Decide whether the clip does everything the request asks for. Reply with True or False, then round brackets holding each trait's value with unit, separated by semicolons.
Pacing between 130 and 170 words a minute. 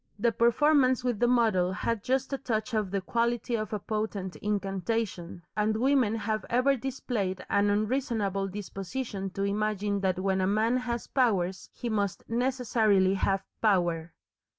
True (150 wpm)